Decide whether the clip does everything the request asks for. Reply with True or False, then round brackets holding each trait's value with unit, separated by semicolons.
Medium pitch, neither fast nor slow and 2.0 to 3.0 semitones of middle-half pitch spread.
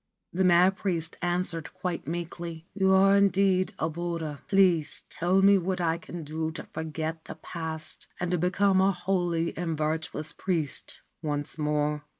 True (170 Hz; 155 wpm; 2.7 semitones)